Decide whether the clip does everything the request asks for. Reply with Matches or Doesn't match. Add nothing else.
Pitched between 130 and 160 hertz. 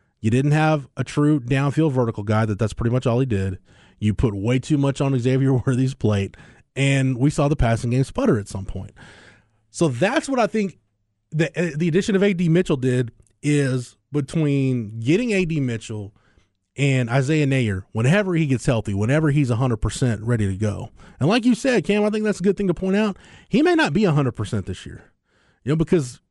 Matches